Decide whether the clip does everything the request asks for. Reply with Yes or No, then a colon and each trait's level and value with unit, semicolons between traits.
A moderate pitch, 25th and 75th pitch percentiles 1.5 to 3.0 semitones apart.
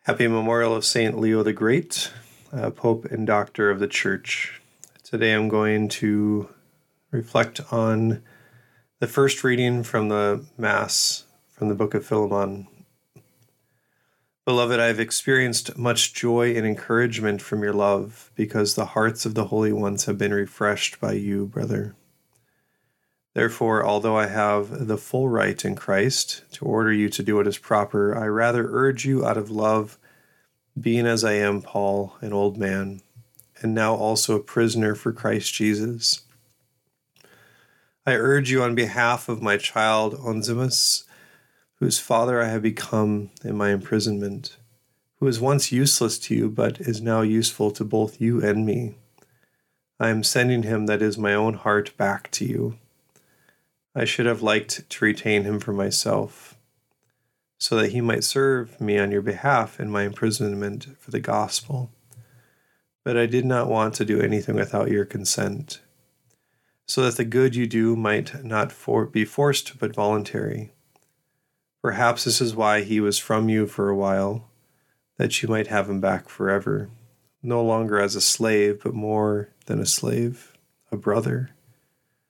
No: low, 110 Hz; average, 2.7 semitones